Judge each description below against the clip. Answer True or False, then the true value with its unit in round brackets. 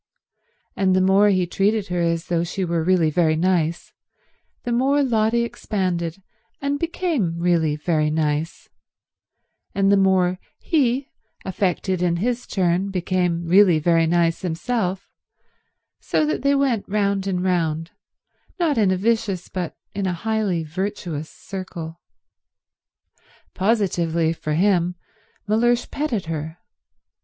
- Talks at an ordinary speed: False (130 wpm)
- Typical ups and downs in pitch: True (3.8 semitones)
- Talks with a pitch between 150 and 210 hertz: True (185 Hz)